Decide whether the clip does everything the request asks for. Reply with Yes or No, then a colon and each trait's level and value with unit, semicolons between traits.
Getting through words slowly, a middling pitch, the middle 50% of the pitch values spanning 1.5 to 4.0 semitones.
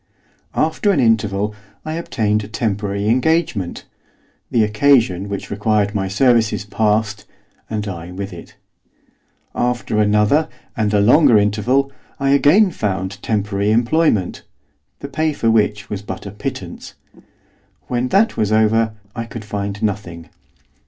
No: slow, 130 wpm; low, 105 Hz; average, 3.3 semitones